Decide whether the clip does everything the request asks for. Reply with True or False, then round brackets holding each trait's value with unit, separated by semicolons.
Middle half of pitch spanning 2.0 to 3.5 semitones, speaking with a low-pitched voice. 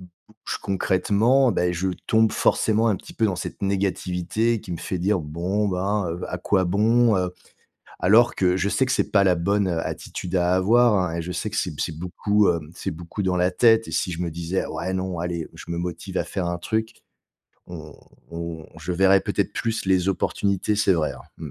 True (3.2 semitones; 95 Hz)